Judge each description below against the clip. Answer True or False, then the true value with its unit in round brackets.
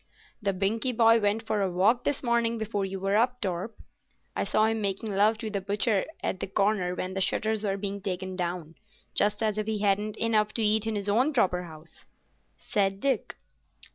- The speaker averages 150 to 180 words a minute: False (200 wpm)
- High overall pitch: True (205 Hz)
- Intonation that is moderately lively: False (2.3 semitones)